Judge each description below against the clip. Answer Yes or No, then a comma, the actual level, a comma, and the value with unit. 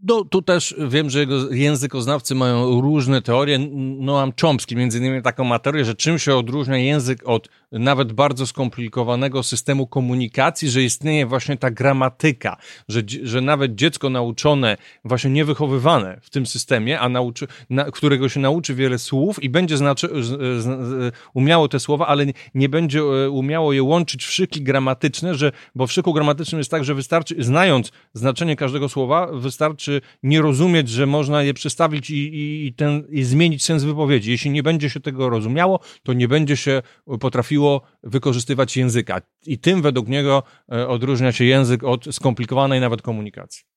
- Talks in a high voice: No, low, 135 Hz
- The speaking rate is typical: No, fast, 165 wpm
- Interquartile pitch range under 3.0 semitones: Yes, narrow, 2.6 semitones